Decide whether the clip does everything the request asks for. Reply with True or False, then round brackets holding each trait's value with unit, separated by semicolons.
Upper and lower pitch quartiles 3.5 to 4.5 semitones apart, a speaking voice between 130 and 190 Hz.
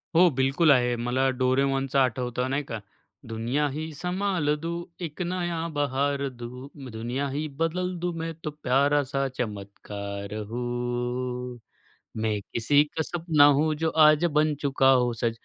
True (4.0 semitones; 135 Hz)